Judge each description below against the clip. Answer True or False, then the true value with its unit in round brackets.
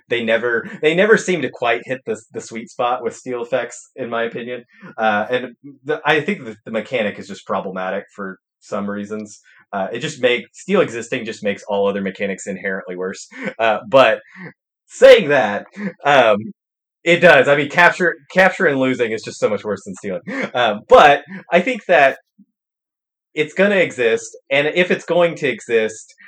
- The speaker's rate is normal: True (185 wpm)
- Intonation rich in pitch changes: True (8.5 semitones)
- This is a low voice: False (145 Hz)